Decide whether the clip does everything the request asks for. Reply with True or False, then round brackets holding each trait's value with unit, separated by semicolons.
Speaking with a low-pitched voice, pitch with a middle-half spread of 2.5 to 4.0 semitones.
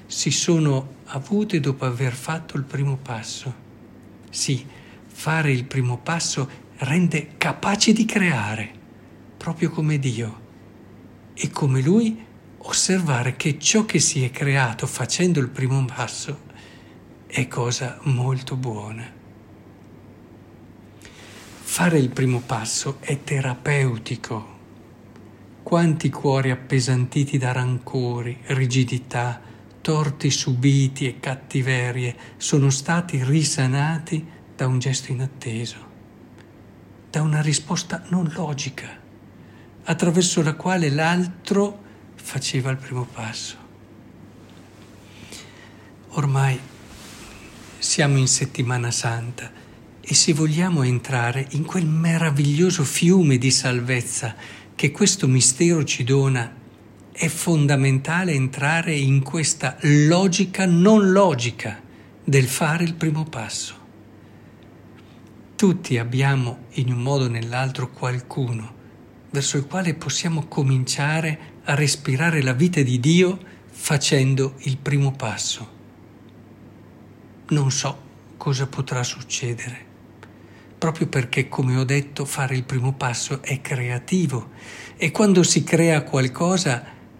False (130 Hz; 4.6 semitones)